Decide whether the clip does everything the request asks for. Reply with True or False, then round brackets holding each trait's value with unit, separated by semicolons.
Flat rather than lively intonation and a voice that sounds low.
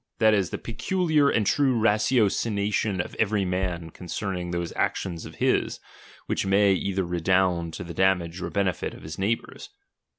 False (3.5 semitones; 95 Hz)